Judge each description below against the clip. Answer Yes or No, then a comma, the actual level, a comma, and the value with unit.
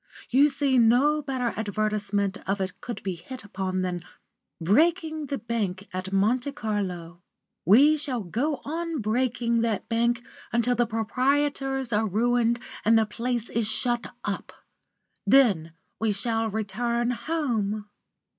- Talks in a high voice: Yes, high, 230 Hz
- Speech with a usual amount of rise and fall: Yes, average, 4.0 semitones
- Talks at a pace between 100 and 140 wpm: Yes, slow, 135 wpm